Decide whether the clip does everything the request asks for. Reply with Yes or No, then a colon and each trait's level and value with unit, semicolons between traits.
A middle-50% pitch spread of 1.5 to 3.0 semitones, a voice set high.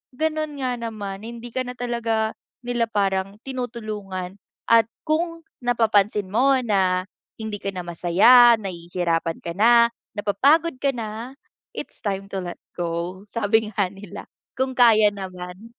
No: average, 4.0 semitones; high, 215 Hz